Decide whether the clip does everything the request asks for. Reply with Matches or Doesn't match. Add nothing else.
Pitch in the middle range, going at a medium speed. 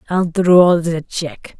Matches